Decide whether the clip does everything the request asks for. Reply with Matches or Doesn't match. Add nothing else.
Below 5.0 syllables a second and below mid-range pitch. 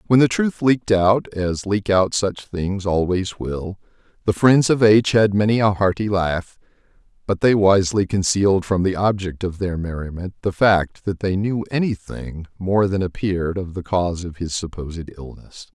Matches